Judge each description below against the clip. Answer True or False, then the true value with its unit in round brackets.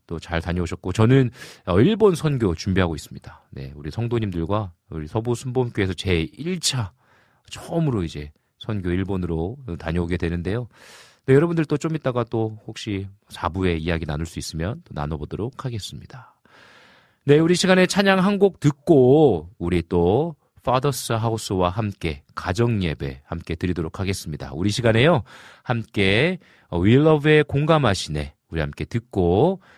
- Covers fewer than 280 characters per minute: False (335 characters per minute)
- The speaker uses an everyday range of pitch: False (7.3 semitones)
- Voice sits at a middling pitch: False (105 Hz)